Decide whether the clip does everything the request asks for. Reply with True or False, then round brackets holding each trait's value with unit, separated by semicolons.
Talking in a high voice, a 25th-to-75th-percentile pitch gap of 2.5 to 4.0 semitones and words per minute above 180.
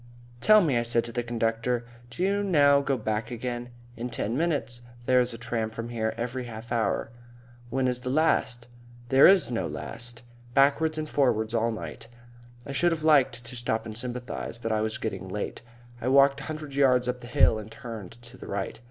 False (120 Hz; 3.2 semitones; 195 wpm)